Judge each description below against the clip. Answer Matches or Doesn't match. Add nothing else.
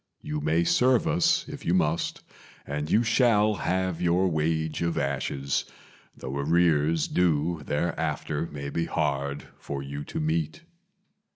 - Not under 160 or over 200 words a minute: Doesn't match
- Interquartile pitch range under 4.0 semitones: Matches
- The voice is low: Matches